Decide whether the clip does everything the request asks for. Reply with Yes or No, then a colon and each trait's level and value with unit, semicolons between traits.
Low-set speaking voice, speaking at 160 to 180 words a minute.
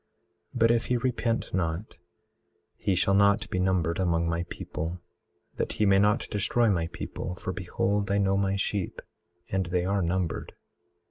Yes: very low, 95 Hz; average, 165 wpm